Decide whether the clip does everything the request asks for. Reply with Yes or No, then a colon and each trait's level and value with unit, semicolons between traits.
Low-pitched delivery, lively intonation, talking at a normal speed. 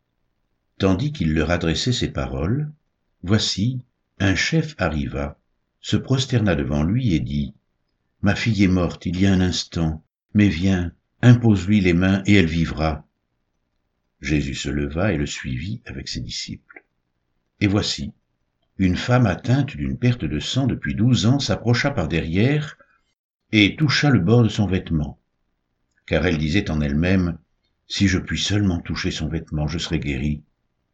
Yes: very low, 85 Hz; wide, 6.3 semitones; average, 155 wpm